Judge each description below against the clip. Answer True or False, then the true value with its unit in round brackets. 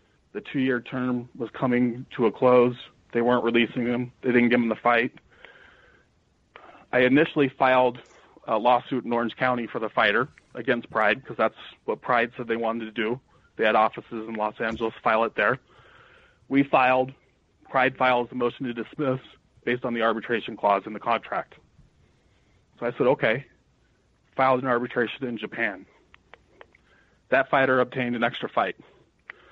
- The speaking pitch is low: True (125 Hz)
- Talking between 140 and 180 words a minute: True (165 wpm)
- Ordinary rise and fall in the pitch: False (1.6 semitones)